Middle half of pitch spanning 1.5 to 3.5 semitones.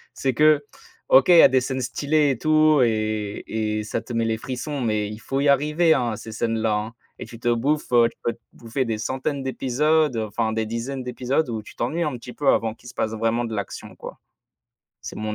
No: average, 3.9 semitones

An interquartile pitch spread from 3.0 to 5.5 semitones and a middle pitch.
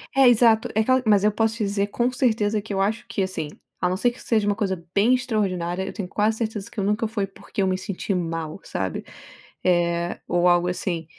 No: average, 3.4 semitones; high, 200 Hz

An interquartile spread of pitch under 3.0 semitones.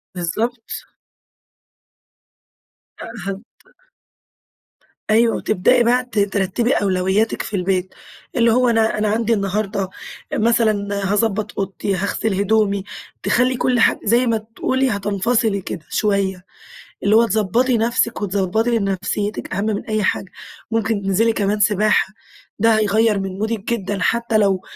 Yes: narrow, 2.5 semitones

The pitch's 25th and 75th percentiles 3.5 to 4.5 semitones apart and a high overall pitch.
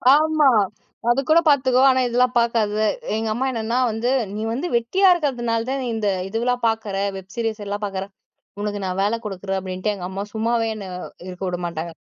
Yes: average, 3.8 semitones; high, 225 Hz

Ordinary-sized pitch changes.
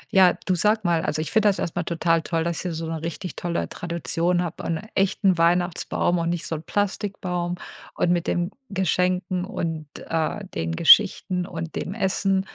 No: narrow, 2.0 semitones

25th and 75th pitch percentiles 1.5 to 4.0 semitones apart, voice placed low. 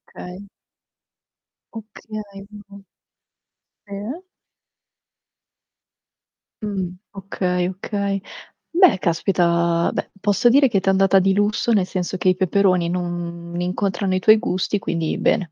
No: narrow, 2.4 semitones; high, 190 Hz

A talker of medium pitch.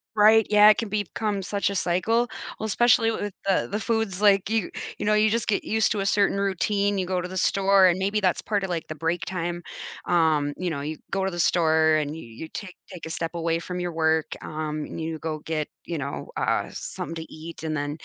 Yes: medium, 180 Hz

